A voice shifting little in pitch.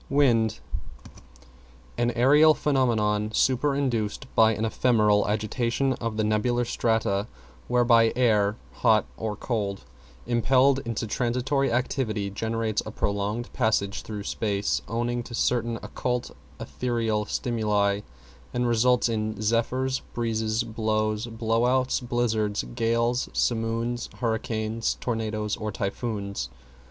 Yes: narrow, 2.1 semitones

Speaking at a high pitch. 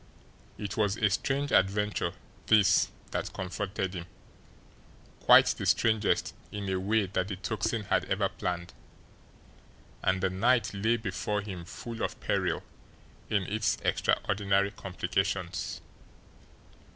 No: low, 100 Hz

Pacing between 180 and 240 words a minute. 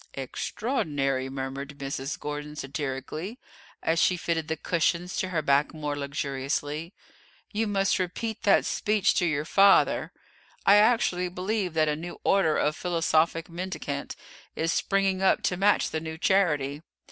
No: average, 145 wpm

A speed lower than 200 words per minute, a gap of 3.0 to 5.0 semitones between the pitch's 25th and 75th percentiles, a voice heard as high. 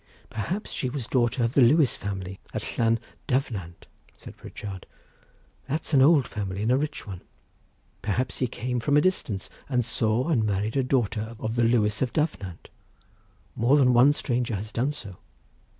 No: average, 170 wpm; average, 4.0 semitones; low, 120 Hz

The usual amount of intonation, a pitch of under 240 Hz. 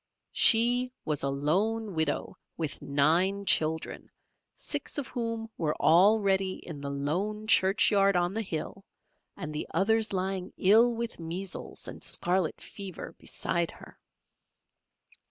Yes: average, 5.0 semitones; high, 190 Hz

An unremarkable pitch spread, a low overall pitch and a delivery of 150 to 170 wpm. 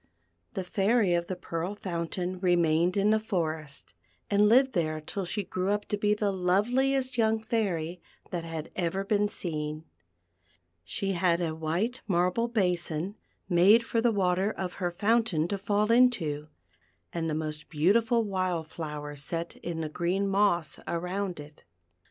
No: average, 3.9 semitones; medium, 185 Hz; average, 155 wpm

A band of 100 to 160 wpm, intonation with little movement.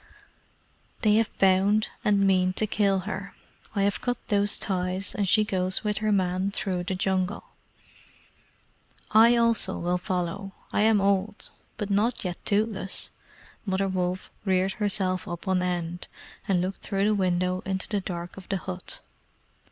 Yes: average, 155 wpm; narrow, 2.0 semitones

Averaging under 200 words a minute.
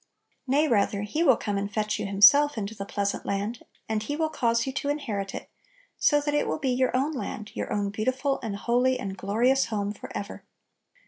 No: fast, 205 wpm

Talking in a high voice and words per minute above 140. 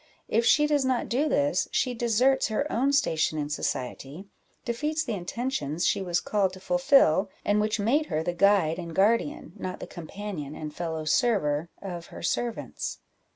Yes: high, 205 Hz; average, 170 wpm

